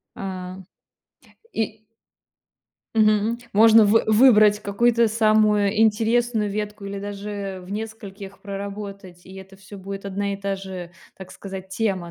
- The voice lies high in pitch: Yes, high, 205 Hz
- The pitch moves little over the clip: Yes, narrow, 1.8 semitones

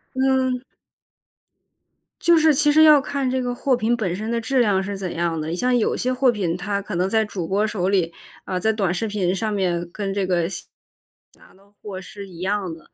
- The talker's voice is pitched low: No, high, 205 Hz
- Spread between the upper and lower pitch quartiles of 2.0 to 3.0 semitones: No, average, 5.1 semitones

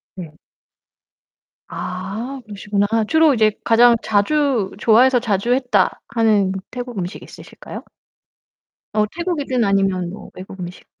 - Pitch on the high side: Yes, high, 215 Hz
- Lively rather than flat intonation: No, average, 4.3 semitones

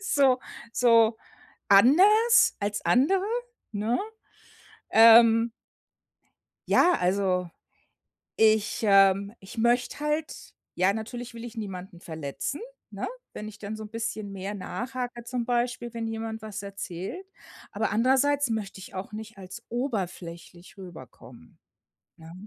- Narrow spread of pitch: No, average, 3.6 semitones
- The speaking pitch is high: Yes, high, 220 Hz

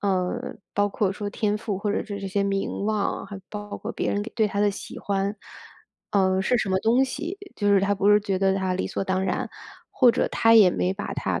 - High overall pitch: Yes, high, 200 Hz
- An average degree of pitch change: No, narrow, 1.5 semitones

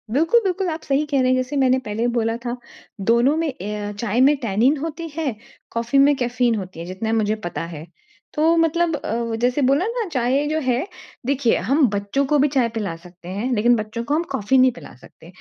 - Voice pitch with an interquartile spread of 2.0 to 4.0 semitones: No, average, 5.1 semitones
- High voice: Yes, very high, 255 Hz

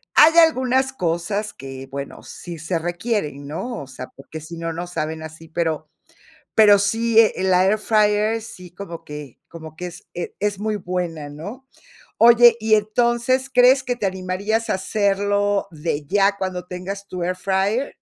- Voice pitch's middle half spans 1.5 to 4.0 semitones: No, average, 4.7 semitones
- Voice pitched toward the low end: No, high, 195 Hz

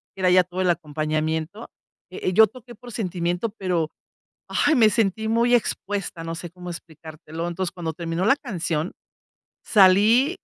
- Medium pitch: Yes, medium, 180 Hz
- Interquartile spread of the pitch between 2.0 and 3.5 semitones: No, average, 4.7 semitones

